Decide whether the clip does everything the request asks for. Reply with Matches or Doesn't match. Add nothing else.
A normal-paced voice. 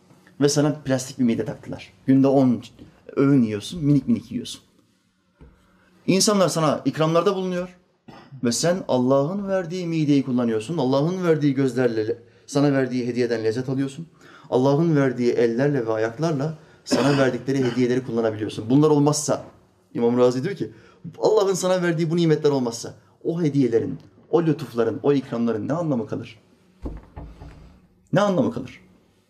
Matches